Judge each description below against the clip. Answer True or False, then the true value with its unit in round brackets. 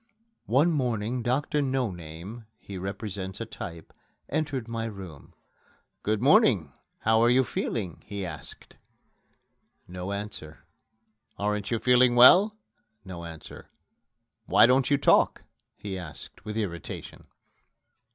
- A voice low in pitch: True (105 Hz)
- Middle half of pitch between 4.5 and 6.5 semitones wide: True (5.1 semitones)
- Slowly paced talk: True (120 wpm)